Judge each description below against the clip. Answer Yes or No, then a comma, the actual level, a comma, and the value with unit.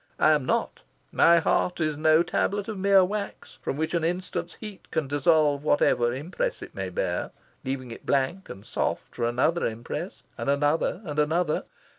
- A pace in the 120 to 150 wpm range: No, average, 175 wpm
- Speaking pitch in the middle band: Yes, medium, 155 Hz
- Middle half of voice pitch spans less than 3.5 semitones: No, average, 4.2 semitones